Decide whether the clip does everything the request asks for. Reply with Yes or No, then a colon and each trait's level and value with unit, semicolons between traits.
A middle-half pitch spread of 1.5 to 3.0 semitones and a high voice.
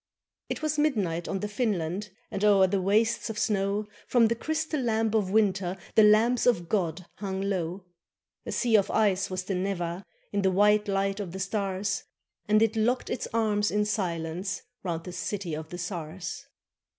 Yes: average, 2.7 semitones; high, 200 Hz